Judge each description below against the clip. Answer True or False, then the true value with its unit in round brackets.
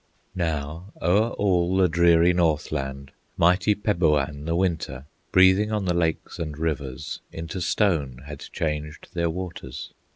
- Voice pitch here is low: True (85 Hz)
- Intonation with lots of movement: False (3.4 semitones)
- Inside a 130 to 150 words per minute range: True (135 wpm)